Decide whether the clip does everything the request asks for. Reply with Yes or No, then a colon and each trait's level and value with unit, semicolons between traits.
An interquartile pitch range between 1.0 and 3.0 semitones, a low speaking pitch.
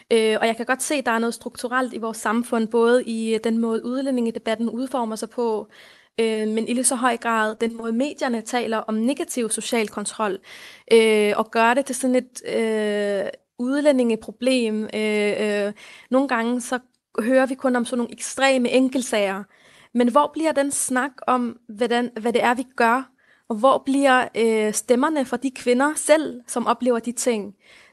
No: narrow, 2.4 semitones; high, 240 Hz